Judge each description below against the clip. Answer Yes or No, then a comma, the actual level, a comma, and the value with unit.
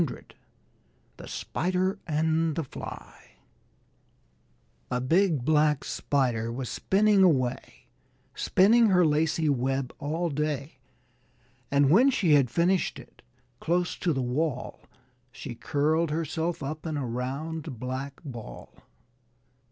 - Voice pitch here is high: No, medium, 150 Hz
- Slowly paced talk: Yes, slow, 115 wpm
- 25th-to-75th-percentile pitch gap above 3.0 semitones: Yes, average, 4.1 semitones